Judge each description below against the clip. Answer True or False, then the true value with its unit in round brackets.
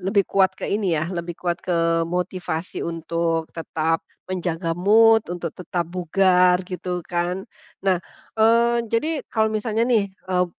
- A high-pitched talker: False (180 Hz)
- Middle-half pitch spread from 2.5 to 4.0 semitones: True (2.9 semitones)